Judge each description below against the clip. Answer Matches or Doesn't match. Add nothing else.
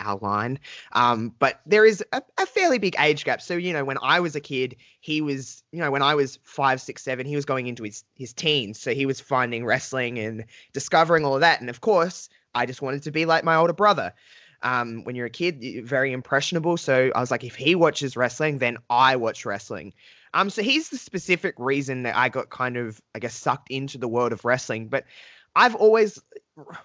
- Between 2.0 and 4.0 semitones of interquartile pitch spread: Doesn't match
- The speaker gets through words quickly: Matches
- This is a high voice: Doesn't match